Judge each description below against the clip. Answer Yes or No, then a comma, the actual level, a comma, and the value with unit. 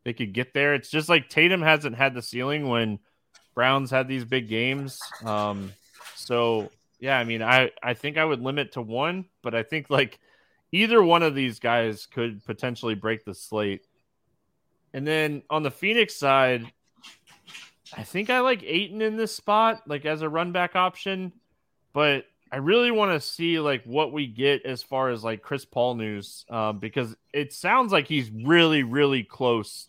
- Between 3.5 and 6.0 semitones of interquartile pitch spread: Yes, average, 5.1 semitones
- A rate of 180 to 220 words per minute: Yes, average, 185 wpm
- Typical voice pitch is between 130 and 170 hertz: Yes, low, 135 Hz